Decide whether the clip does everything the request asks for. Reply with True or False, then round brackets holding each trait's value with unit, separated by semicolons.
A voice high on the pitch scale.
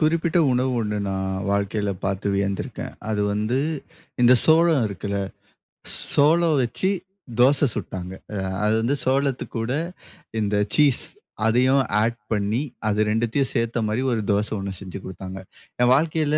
False (115 Hz)